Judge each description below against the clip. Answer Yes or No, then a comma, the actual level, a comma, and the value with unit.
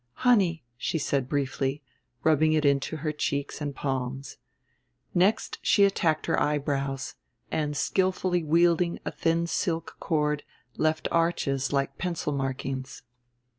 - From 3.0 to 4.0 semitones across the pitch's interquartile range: Yes, average, 3.4 semitones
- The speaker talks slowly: Yes, slow, 125 wpm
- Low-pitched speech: No, medium, 150 Hz